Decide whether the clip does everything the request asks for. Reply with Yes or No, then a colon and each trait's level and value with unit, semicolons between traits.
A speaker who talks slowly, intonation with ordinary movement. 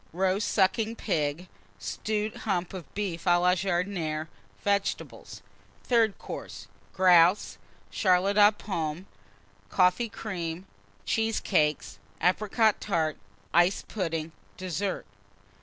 Yes: slow, 95 wpm; average, 3.1 semitones